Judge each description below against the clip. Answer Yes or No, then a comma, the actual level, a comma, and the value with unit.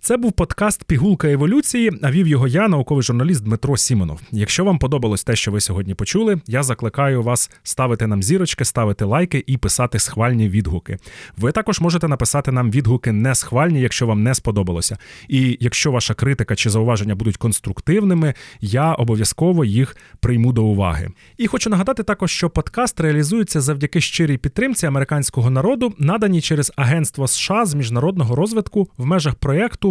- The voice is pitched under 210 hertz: Yes, medium, 140 Hz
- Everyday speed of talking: No, fast, 165 wpm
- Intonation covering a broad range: Yes, wide, 6.9 semitones